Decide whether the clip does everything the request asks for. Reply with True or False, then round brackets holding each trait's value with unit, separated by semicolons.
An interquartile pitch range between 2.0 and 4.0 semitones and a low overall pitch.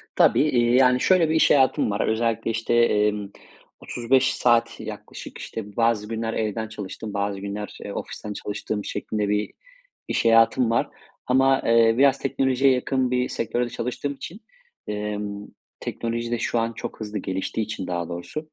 True (3.3 semitones; 115 Hz)